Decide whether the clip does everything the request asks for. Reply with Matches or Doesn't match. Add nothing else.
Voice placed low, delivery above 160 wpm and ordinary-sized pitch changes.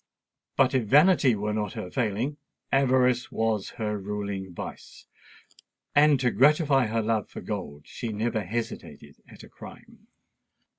Doesn't match